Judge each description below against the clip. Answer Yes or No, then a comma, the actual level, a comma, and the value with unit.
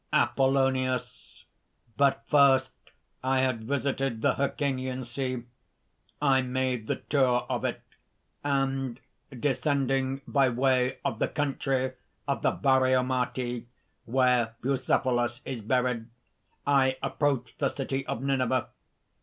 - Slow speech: Yes, slow, 110 wpm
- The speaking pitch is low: Yes, low, 130 Hz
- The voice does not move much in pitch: Yes, narrow, 1.4 semitones